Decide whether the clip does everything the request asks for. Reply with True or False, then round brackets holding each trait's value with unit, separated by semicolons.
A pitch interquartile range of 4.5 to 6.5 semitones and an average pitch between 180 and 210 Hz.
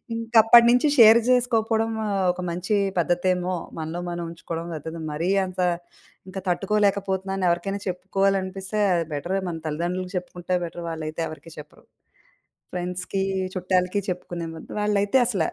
False (2.8 semitones; 185 Hz)